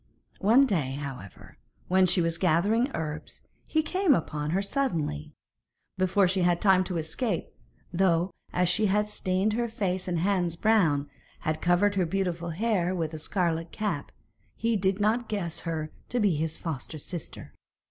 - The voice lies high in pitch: No, medium, 180 Hz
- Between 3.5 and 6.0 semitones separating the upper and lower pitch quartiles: Yes, average, 4.0 semitones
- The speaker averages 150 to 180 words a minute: Yes, average, 160 wpm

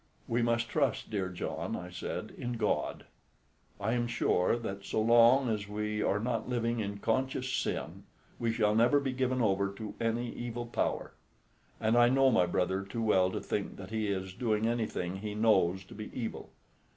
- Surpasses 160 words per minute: Yes, average, 185 wpm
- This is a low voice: Yes, low, 110 Hz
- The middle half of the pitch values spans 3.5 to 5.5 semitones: No, average, 3.1 semitones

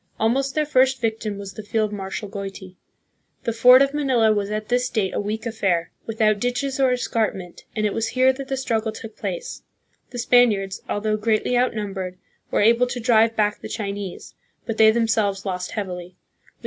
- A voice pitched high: Yes, high, 220 Hz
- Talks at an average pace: Yes, average, 185 wpm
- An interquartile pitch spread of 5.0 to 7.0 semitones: No, average, 3.4 semitones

